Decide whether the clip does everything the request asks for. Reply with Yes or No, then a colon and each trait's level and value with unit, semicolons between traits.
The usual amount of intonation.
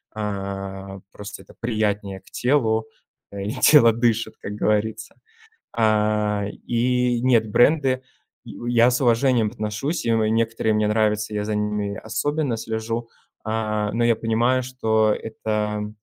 No: narrow, 2.0 semitones